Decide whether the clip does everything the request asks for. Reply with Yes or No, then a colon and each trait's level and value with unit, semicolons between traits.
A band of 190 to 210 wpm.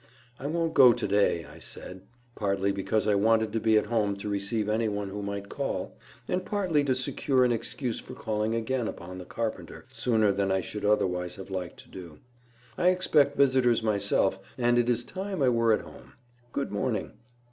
Yes: average, 195 wpm